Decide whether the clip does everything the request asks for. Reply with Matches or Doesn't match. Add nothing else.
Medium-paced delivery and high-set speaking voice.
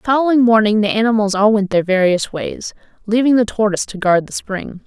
Doesn't match